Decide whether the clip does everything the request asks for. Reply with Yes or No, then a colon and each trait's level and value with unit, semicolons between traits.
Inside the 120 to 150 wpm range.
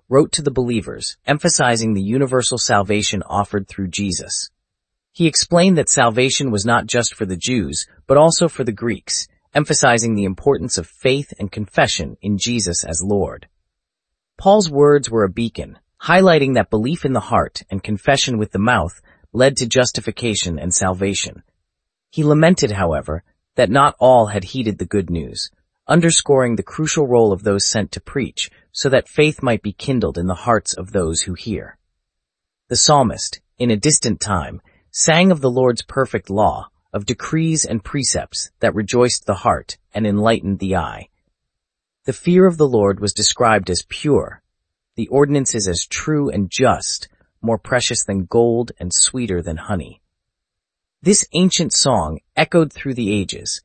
No: average, 160 wpm